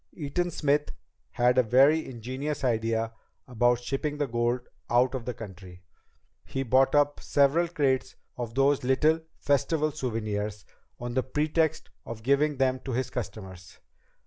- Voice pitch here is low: Yes, low, 130 Hz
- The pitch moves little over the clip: No, average, 3.7 semitones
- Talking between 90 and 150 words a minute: Yes, average, 145 wpm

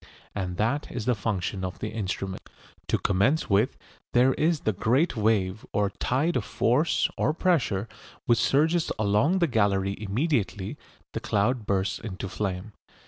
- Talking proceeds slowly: No, average, 150 wpm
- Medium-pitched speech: No, low, 110 Hz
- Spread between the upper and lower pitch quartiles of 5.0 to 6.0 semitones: Yes, average, 5.3 semitones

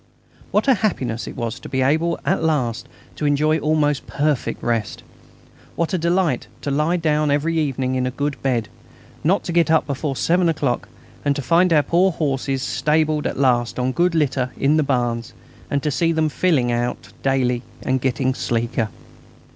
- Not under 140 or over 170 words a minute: No, average, 180 wpm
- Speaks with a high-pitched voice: No, medium, 145 Hz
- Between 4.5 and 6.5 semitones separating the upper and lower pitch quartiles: No, average, 3.9 semitones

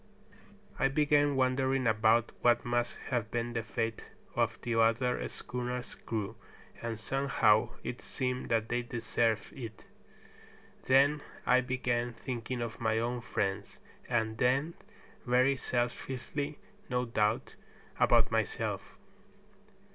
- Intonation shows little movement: Yes, narrow, 2.2 semitones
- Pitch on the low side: Yes, low, 120 Hz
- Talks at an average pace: No, slow, 115 wpm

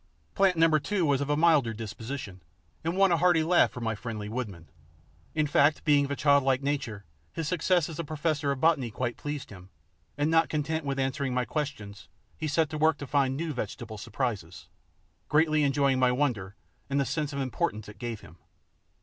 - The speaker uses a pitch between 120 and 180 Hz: Yes, medium, 140 Hz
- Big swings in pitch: No, average, 4.5 semitones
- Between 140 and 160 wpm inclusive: No, average, 190 wpm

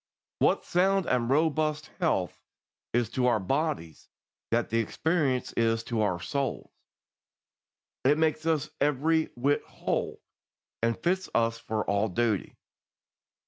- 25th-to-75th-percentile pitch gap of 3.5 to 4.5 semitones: No, average, 5.3 semitones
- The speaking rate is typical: No, slow, 125 wpm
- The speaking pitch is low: Yes, low, 130 Hz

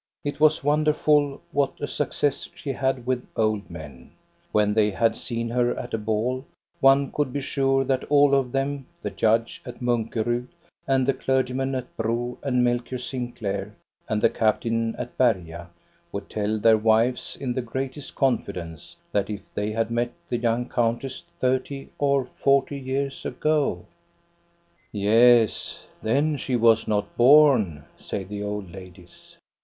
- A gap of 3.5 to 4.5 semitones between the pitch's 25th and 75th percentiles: Yes, average, 3.8 semitones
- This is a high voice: No, low, 120 Hz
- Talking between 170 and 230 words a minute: No, average, 155 wpm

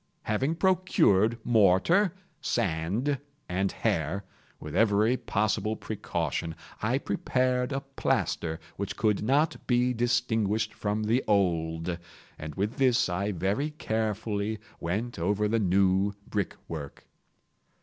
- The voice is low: Yes, low, 105 Hz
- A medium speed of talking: No, slow, 110 wpm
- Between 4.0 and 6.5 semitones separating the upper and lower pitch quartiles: Yes, average, 4.3 semitones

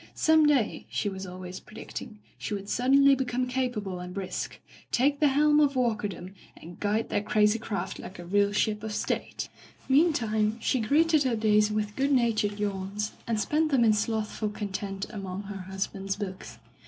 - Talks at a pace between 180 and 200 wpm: Yes, average, 190 wpm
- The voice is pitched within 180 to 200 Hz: No, high, 215 Hz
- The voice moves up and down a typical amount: Yes, average, 4.2 semitones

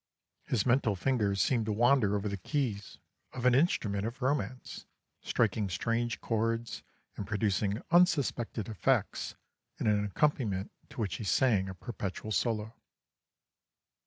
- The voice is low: Yes, low, 110 Hz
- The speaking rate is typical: No, slow, 130 wpm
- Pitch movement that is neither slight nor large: Yes, average, 3.4 semitones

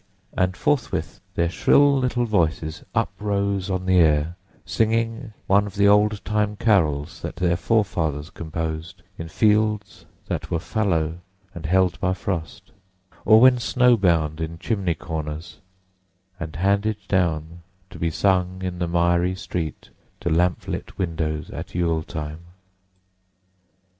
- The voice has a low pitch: Yes, very low, 90 Hz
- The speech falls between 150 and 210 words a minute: No, slow, 135 wpm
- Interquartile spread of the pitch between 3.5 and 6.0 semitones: Yes, average, 3.9 semitones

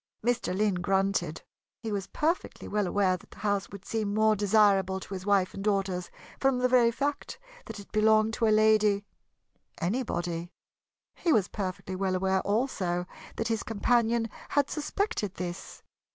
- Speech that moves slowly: No, average, 160 wpm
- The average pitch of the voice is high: Yes, high, 205 Hz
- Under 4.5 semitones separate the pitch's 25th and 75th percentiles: Yes, average, 2.9 semitones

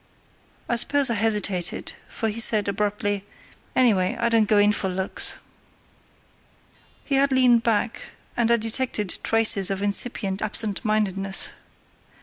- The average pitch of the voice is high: Yes, high, 215 Hz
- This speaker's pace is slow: Yes, slow, 130 wpm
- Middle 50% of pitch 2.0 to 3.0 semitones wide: Yes, average, 2.7 semitones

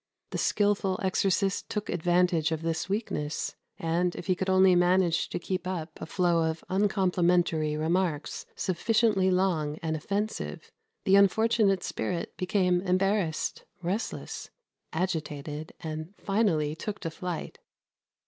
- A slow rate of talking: Yes, slow, 125 wpm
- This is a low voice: No, medium, 180 Hz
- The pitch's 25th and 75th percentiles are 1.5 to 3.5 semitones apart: Yes, average, 3.1 semitones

